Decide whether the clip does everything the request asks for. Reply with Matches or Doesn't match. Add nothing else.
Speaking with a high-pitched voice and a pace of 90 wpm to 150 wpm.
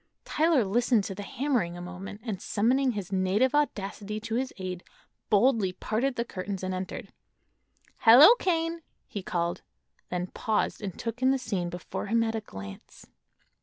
Doesn't match